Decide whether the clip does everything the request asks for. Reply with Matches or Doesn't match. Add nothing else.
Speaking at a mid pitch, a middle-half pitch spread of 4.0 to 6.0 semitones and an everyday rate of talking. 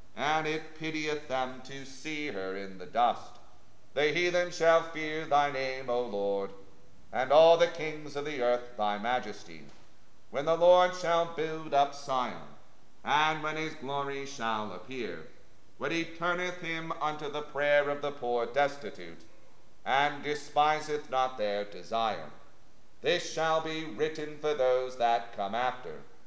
Matches